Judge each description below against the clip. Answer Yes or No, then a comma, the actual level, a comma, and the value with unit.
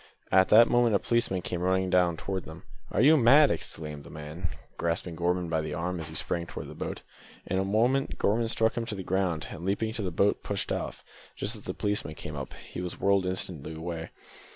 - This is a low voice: Yes, very low, 90 Hz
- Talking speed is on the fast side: Yes, fast, 225 wpm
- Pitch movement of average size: Yes, average, 4.0 semitones